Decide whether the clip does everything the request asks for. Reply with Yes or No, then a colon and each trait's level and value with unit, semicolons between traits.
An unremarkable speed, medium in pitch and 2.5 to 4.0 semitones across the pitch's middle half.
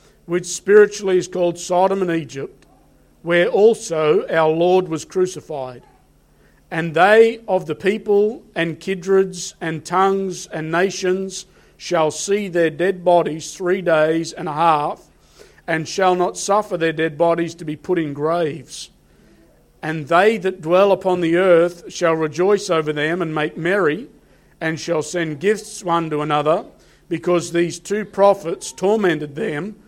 Yes: average, 145 wpm; medium, 175 Hz; average, 2.9 semitones